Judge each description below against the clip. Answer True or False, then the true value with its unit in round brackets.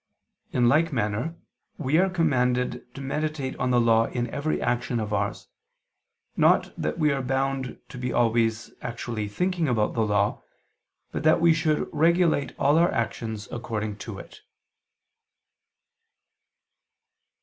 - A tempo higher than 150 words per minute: False (140 wpm)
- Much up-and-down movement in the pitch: False (5.0 semitones)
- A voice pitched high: False (125 Hz)